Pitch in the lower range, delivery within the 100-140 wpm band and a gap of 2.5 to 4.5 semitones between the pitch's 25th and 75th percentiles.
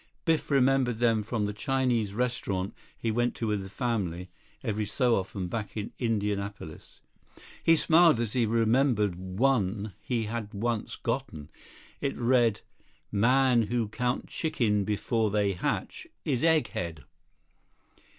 Yes: low, 115 Hz; slow, 135 wpm; average, 3.5 semitones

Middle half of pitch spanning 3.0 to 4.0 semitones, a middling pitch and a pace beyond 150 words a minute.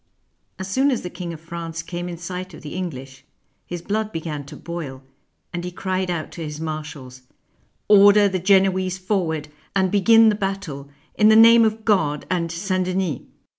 Yes: average, 3.5 semitones; medium, 180 Hz; average, 185 wpm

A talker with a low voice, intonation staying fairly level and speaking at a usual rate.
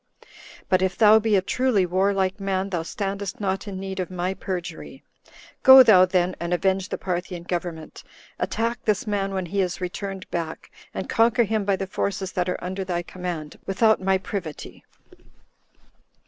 No: high, 190 Hz; narrow, 1.9 semitones; average, 170 wpm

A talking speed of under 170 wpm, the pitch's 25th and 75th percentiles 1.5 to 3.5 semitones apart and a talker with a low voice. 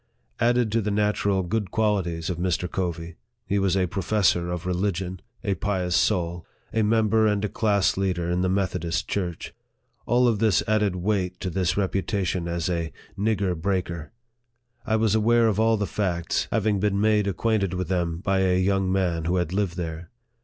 No: average, 190 wpm; average, 3.0 semitones; very low, 95 Hz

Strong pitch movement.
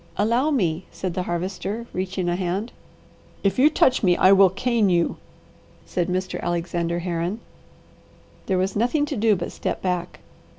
No: average, 3.6 semitones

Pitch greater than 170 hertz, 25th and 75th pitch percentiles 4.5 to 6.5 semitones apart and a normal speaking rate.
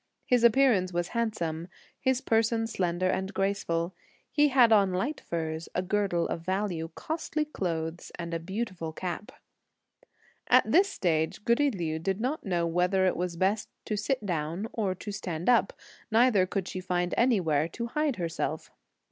Yes: high, 190 Hz; average, 5.0 semitones; average, 160 wpm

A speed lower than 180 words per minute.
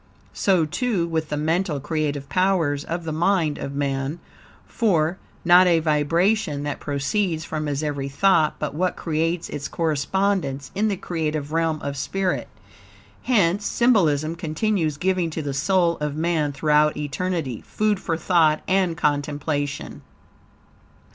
Yes: average, 140 wpm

